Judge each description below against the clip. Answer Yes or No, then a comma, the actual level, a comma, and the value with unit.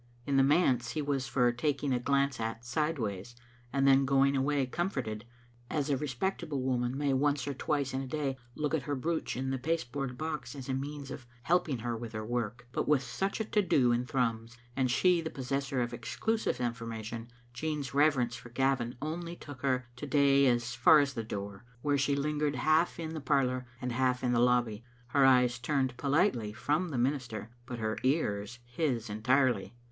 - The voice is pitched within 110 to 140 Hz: Yes, low, 135 Hz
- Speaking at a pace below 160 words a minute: No, fast, 205 wpm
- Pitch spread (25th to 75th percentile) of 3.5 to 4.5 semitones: No, average, 3.1 semitones